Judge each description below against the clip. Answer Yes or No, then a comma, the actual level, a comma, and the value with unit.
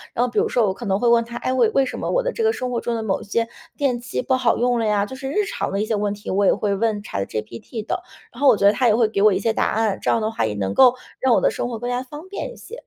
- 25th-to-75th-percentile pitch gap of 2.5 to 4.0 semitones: Yes, average, 3.6 semitones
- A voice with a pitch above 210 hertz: Yes, high, 230 Hz